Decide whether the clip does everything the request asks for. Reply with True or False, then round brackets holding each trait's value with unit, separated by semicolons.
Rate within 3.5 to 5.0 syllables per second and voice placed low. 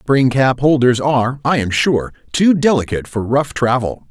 True (4.7 syllables/s; 130 Hz)